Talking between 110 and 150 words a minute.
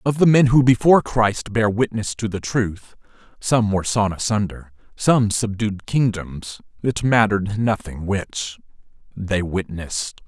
Yes: average, 140 wpm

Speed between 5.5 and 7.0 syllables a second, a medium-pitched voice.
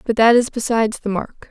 No: 5.8 syllables/s; high, 225 Hz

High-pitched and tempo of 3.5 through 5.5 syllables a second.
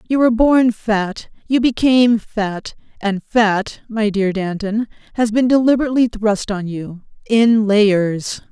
Yes: high, 220 Hz; 4.0 syllables/s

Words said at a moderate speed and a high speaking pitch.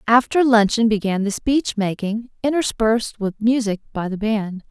Yes: average, 155 wpm; high, 220 Hz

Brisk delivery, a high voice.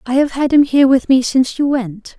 Yes: fast, 275 wpm; very high, 260 Hz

